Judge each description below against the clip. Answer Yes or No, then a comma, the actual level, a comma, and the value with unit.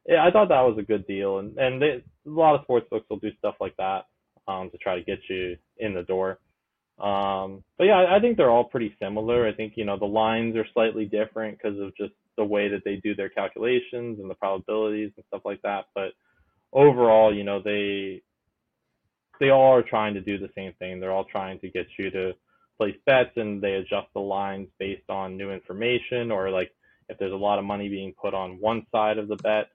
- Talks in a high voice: No, low, 105 Hz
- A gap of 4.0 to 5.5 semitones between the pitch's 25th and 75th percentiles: No, narrow, 2.6 semitones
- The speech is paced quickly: Yes, fast, 230 wpm